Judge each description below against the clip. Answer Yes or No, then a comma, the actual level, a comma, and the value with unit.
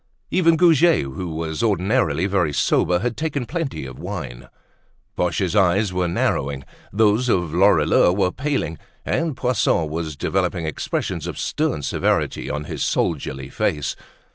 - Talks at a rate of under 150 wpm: Yes, average, 140 wpm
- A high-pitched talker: No, very low, 90 Hz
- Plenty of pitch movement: Yes, wide, 7.4 semitones